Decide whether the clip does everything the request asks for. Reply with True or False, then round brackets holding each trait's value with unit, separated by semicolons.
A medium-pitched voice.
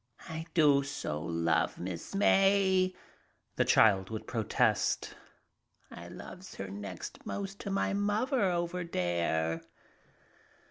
True (150 Hz)